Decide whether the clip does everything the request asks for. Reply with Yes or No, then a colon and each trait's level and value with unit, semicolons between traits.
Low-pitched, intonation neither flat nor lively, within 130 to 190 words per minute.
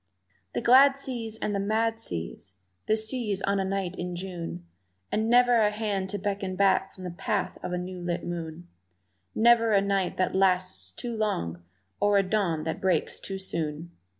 No: high, 195 Hz; average, 3.5 semitones; average, 180 wpm